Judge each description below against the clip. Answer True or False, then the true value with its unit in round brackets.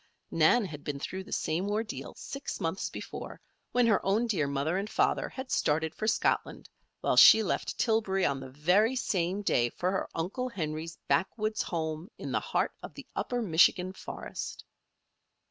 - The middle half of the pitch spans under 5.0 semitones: False (5.4 semitones)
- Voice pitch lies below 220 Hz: True (190 Hz)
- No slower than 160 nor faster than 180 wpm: True (170 wpm)